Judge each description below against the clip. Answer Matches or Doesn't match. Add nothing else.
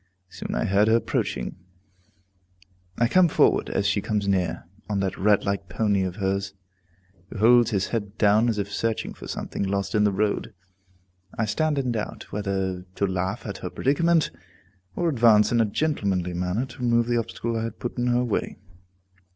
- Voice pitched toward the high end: Doesn't match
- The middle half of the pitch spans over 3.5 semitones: Doesn't match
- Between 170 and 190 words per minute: Matches